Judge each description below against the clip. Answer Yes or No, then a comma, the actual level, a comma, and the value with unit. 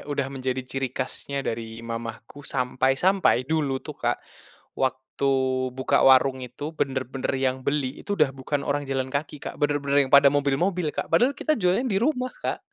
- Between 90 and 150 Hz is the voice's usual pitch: Yes, medium, 140 Hz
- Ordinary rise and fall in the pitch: No, narrow, 2.2 semitones